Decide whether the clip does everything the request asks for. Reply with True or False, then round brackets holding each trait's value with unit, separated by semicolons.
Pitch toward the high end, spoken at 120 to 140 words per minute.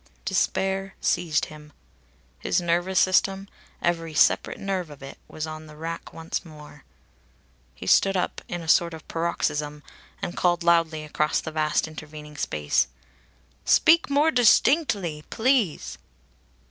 False (165 Hz; 135 wpm)